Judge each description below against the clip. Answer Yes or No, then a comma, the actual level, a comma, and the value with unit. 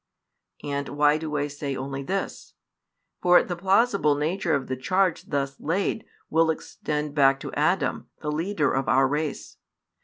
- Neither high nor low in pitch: Yes, medium, 150 Hz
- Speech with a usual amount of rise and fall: Yes, average, 3.8 semitones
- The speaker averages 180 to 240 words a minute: No, average, 155 wpm